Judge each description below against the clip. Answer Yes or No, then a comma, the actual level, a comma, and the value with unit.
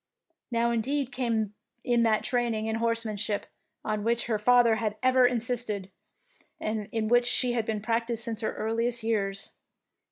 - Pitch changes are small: Yes, narrow, 1.9 semitones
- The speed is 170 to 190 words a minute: No, average, 155 wpm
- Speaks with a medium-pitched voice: No, high, 230 Hz